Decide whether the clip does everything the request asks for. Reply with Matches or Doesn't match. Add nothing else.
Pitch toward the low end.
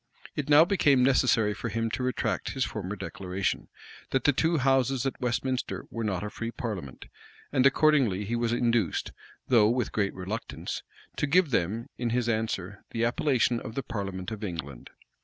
Matches